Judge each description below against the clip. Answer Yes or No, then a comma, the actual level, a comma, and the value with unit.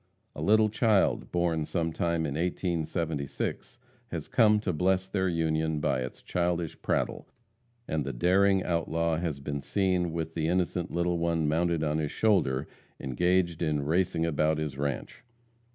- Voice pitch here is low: Yes, very low, 85 Hz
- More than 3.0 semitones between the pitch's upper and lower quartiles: No, average, 2.7 semitones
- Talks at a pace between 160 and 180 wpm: No, average, 150 wpm